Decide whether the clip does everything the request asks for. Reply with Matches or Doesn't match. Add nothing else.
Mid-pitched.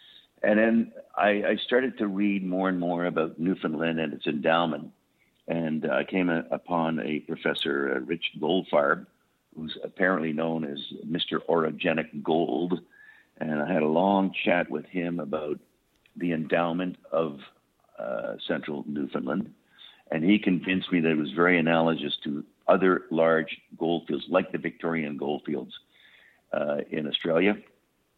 Doesn't match